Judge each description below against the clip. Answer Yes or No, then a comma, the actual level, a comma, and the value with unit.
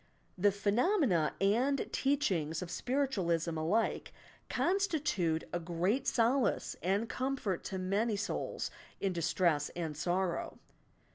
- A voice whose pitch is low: No, high, 195 Hz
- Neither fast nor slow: No, slow, 110 wpm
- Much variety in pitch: Yes, wide, 6.9 semitones